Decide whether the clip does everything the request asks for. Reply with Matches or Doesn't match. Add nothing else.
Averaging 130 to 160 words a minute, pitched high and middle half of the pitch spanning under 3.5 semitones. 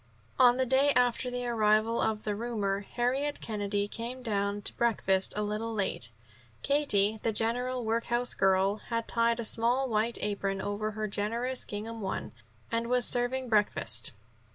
Matches